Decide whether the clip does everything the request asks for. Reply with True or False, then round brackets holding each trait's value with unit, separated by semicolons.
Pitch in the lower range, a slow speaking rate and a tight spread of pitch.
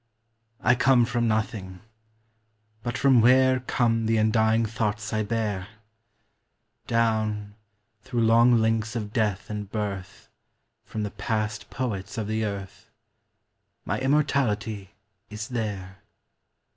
True (110 Hz; 115 wpm; 2.2 semitones)